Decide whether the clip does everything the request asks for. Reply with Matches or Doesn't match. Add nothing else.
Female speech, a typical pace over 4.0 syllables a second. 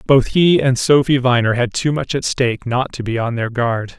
Doesn't match